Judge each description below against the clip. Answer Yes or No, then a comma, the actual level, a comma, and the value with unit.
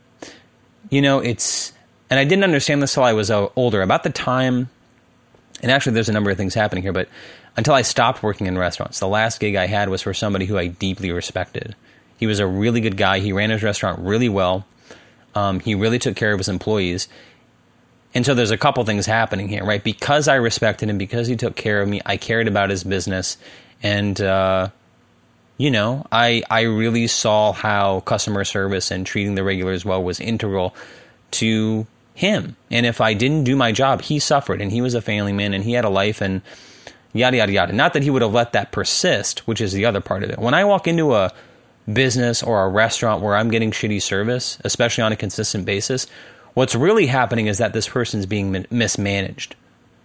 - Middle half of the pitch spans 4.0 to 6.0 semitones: No, average, 3.6 semitones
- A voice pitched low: Yes, low, 110 Hz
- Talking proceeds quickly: Yes, fast, 210 wpm